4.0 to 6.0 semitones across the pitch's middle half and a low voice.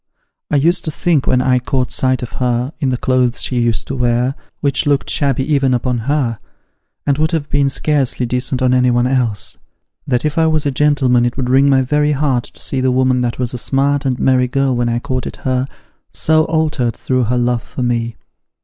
No: narrow, 2.4 semitones; low, 130 Hz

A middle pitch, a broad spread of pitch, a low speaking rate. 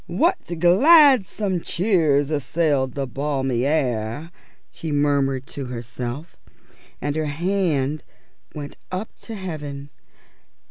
No: medium, 150 Hz; average, 4.5 semitones; slow, 100 wpm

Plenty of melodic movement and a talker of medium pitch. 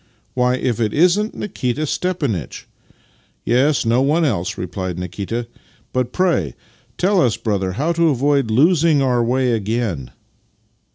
No: wide, 6.0 semitones; low, 125 Hz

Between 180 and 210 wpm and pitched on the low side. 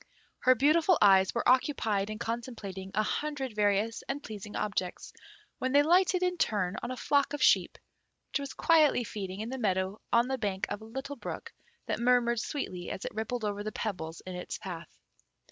No: average, 190 wpm; high, 225 Hz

